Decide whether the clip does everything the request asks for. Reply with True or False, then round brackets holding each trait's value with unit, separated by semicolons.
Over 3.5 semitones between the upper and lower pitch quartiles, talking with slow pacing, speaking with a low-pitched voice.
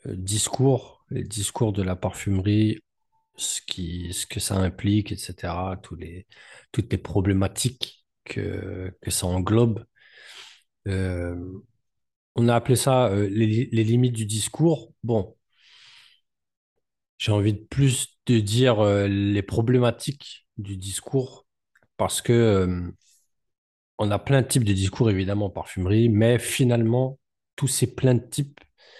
True (4.1 semitones; 135 wpm; 110 Hz)